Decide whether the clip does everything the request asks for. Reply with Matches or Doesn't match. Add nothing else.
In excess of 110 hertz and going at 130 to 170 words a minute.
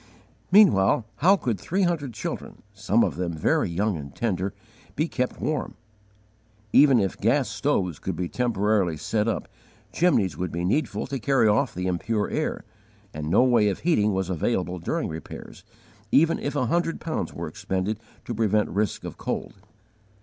Doesn't match